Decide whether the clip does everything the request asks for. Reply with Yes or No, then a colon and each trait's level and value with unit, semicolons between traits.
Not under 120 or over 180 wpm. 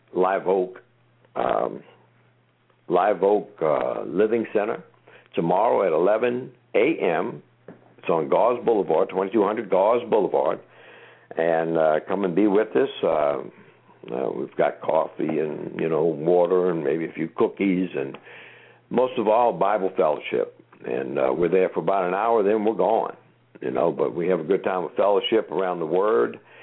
Yes: average, 160 wpm